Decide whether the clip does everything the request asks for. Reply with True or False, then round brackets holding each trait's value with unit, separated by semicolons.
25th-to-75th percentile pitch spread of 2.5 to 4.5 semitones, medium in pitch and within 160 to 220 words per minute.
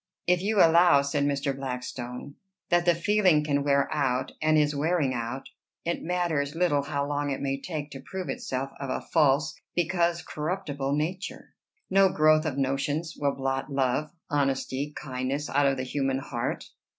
True (3.2 semitones; 145 Hz; 165 wpm)